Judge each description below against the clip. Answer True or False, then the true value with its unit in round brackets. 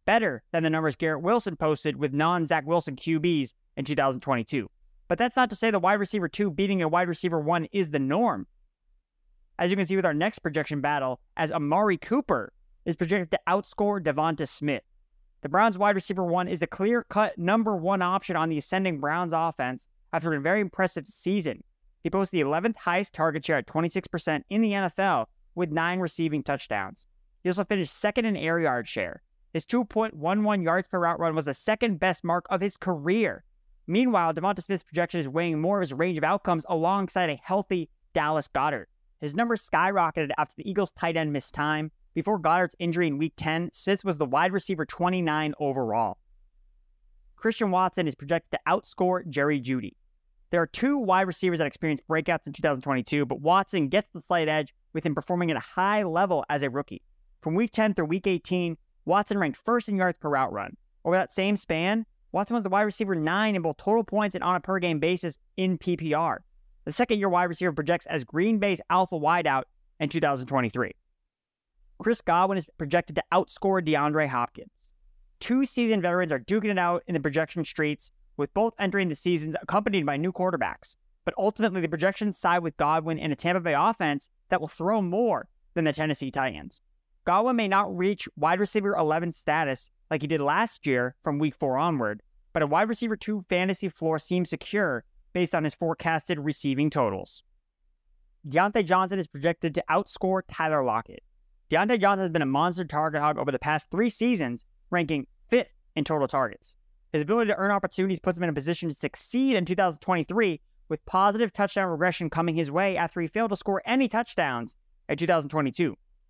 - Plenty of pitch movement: False (4.2 semitones)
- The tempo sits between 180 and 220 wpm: True (190 wpm)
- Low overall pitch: False (175 Hz)